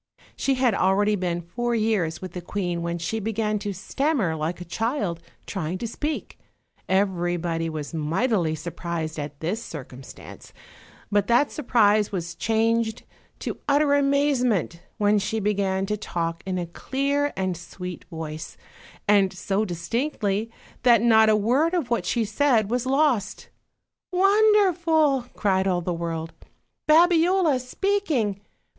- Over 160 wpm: No, average, 140 wpm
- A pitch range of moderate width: No, wide, 6.5 semitones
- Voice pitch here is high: Yes, high, 205 Hz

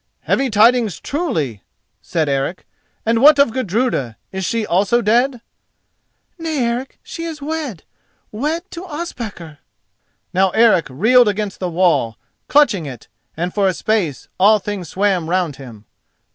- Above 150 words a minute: No, slow, 135 wpm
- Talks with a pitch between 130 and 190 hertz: No, high, 210 Hz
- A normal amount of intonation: No, wide, 6.7 semitones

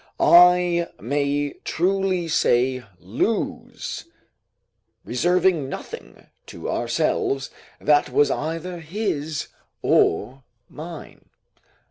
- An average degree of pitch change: Yes, average, 3.9 semitones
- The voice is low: No, medium, 155 Hz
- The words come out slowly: Yes, slow, 75 wpm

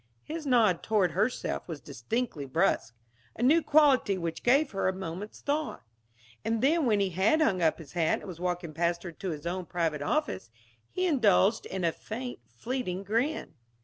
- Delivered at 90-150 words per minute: No, average, 180 wpm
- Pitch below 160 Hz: No, high, 195 Hz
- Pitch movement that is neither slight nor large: No, wide, 6.8 semitones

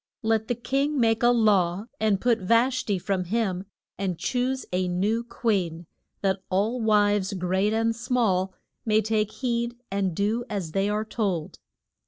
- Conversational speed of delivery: Yes, average, 160 wpm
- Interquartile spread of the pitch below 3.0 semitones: No, average, 3.5 semitones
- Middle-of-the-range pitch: No, high, 215 Hz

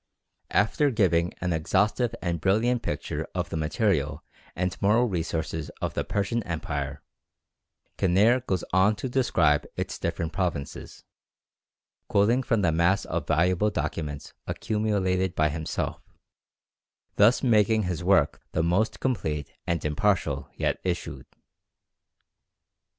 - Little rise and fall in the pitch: No, average, 4.7 semitones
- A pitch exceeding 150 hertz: No, very low, 90 Hz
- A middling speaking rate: No, slow, 120 wpm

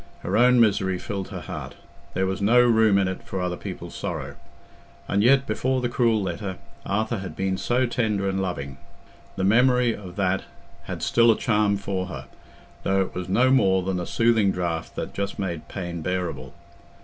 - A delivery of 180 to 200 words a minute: Yes, average, 185 wpm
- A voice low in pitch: Yes, low, 100 Hz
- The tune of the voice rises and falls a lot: No, average, 3.6 semitones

